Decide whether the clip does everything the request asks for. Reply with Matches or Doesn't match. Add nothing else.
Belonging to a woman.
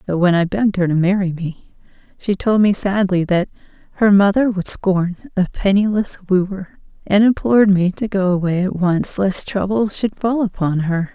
Matches